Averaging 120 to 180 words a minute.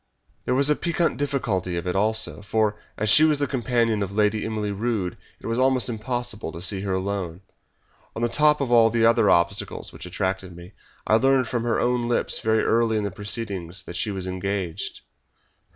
No: average, 200 wpm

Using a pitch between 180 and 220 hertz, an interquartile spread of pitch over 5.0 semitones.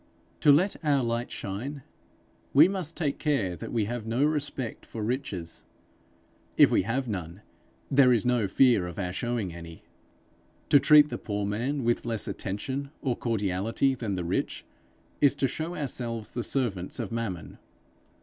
No: low, 120 Hz; wide, 5.5 semitones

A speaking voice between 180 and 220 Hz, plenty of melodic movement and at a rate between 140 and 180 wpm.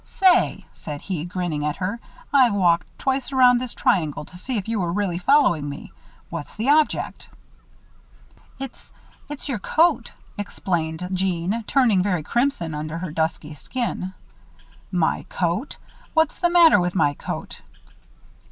Yes: high, 190 Hz; wide, 7.5 semitones; average, 145 wpm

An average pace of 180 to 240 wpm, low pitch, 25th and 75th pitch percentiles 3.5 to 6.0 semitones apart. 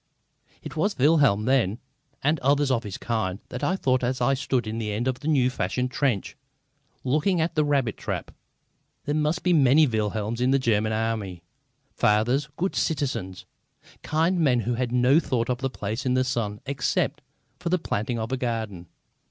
Yes: average, 185 wpm; low, 125 Hz; average, 4.4 semitones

